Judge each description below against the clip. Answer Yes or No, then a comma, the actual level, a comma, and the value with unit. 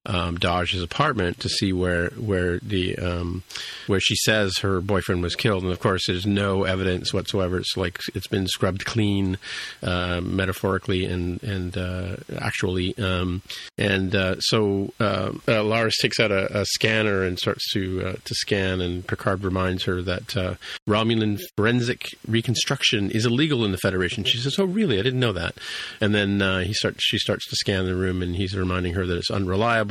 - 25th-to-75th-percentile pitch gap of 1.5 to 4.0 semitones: Yes, average, 2.9 semitones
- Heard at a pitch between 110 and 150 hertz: No, very low, 95 Hz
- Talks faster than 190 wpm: No, average, 185 wpm